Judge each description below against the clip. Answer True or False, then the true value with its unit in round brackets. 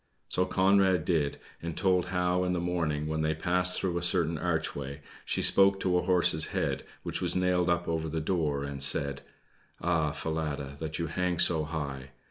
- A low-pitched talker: True (85 Hz)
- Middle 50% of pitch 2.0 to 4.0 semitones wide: True (2.8 semitones)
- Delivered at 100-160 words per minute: False (185 wpm)